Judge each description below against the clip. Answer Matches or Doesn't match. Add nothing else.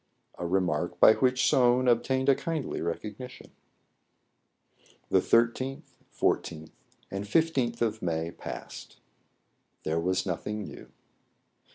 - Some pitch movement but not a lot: Doesn't match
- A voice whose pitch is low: Matches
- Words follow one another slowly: Matches